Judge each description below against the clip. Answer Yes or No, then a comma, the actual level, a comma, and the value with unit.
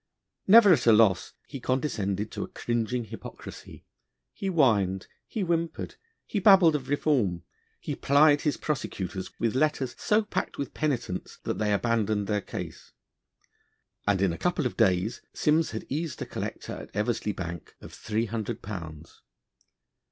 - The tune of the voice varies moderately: No, wide, 6.9 semitones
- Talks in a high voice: No, low, 115 Hz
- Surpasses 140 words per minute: Yes, average, 150 wpm